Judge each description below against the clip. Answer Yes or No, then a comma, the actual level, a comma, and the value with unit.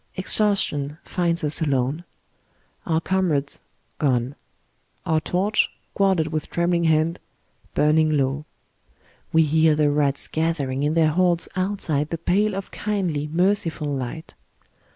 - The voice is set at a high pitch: No, medium, 160 Hz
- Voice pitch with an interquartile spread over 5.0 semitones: No, average, 3.2 semitones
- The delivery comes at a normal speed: No, slow, 120 wpm